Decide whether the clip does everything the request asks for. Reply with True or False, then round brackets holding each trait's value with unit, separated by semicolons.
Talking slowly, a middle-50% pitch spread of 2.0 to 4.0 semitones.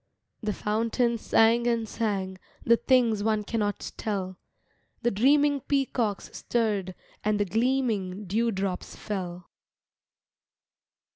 True (110 wpm; 3.0 semitones)